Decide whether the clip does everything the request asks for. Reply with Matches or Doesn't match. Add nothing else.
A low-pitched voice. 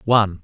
Matches